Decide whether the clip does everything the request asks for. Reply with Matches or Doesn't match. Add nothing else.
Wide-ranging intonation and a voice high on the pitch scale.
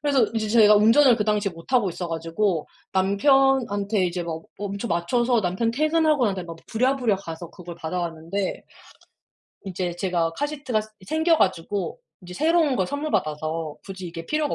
Matches